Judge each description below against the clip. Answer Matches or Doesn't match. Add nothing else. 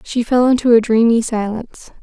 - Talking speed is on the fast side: Doesn't match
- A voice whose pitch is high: Matches